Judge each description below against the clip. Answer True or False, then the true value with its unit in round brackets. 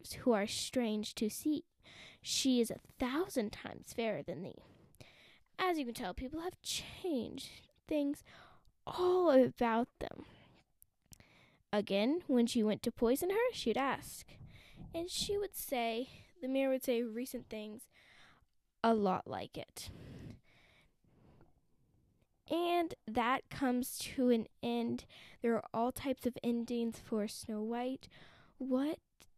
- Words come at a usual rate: False (130 wpm)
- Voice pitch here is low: False (245 Hz)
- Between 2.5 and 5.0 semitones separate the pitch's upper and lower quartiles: True (3.8 semitones)